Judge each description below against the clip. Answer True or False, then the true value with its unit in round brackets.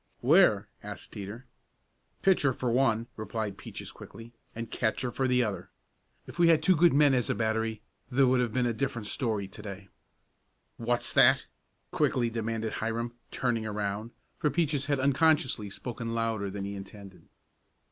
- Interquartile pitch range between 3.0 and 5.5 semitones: True (3.4 semitones)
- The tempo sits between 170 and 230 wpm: False (160 wpm)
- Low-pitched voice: True (115 Hz)